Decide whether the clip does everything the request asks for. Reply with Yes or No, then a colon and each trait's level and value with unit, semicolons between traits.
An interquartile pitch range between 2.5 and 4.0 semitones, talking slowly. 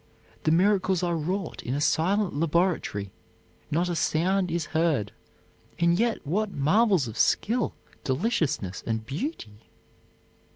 No: average, 5.1 semitones; slow, 125 wpm